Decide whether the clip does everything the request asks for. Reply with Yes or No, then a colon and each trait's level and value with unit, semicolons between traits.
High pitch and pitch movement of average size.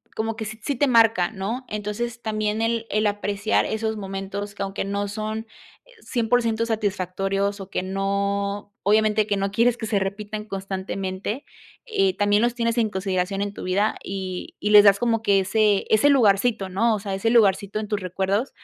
No: high, 205 Hz; narrow, 2.3 semitones